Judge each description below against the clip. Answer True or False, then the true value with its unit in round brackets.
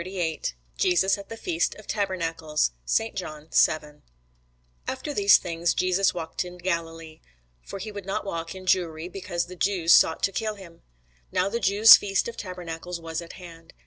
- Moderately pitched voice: True (180 Hz)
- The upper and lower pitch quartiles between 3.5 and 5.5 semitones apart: False (3.0 semitones)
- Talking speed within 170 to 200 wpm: True (180 wpm)